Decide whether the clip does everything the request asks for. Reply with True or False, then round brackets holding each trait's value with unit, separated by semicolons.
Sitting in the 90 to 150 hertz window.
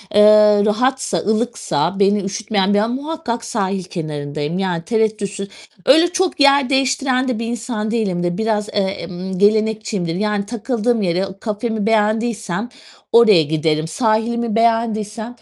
False (215 Hz)